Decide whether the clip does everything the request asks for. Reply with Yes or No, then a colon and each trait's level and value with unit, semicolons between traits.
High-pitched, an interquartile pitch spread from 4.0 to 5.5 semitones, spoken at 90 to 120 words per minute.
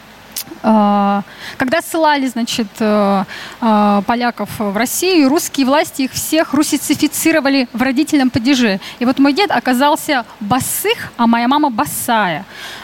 Yes: very high, 265 Hz; average, 4.4 semitones; slow, 110 wpm